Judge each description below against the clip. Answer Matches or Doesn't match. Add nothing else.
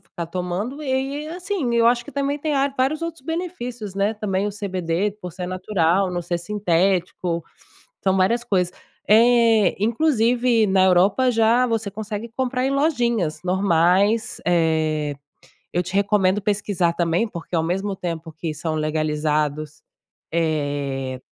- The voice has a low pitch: Doesn't match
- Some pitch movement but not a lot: Doesn't match